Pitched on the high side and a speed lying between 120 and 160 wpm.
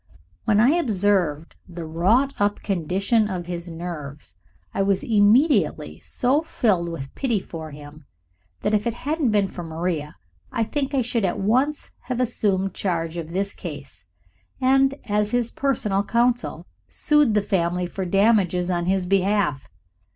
Yes: high, 195 Hz; average, 150 wpm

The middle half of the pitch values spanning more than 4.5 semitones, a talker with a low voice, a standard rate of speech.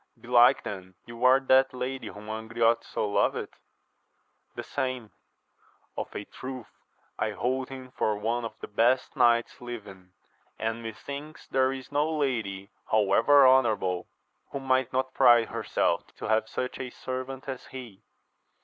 No: average, 3.0 semitones; low, 125 Hz; average, 155 wpm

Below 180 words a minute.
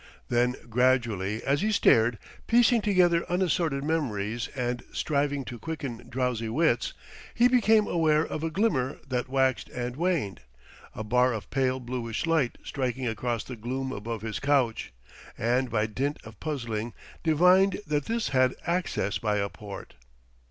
Yes: average, 150 wpm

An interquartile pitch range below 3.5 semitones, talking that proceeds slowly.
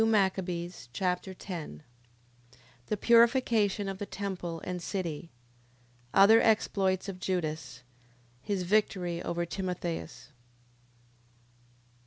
Yes: average, 2.7 semitones; slow, 95 wpm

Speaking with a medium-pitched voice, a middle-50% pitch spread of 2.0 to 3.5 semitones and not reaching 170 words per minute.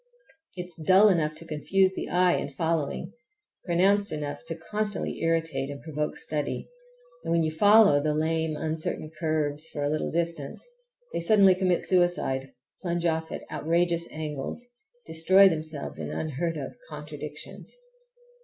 Yes: medium, 165 Hz; narrow, 2.6 semitones; average, 145 wpm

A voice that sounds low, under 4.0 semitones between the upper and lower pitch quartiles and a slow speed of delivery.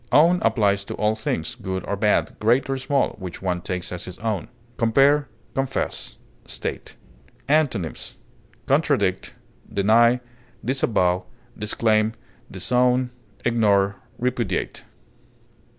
No: low, 110 Hz; average, 4.3 semitones; slow, 105 wpm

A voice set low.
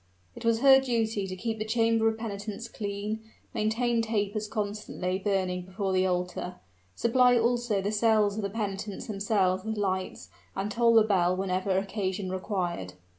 No: high, 205 Hz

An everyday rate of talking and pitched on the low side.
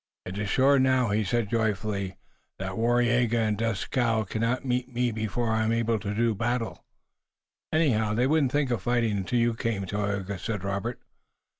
Yes: average, 165 wpm; low, 115 Hz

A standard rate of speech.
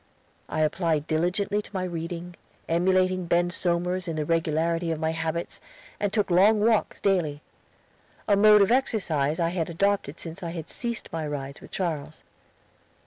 Yes: average, 160 wpm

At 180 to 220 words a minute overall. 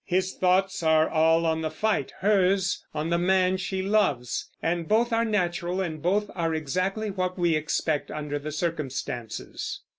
No: average, 160 wpm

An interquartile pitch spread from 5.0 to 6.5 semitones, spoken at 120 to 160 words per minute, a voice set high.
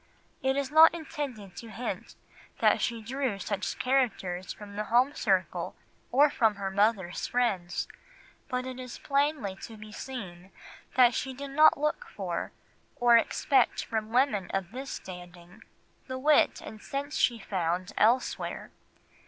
Yes: average, 5.3 semitones; average, 145 wpm; high, 235 Hz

